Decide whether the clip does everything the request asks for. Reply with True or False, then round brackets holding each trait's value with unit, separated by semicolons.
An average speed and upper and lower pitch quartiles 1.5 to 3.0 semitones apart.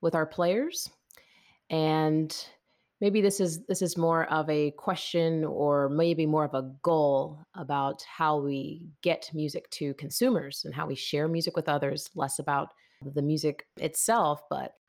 True (155 wpm; 2.5 semitones)